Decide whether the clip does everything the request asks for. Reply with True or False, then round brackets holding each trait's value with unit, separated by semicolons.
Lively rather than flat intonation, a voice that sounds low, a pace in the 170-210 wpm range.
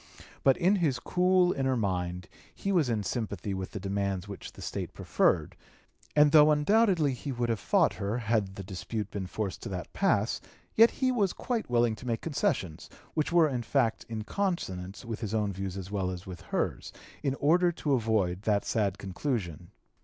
True (7.3 semitones; 115 Hz; 190 wpm)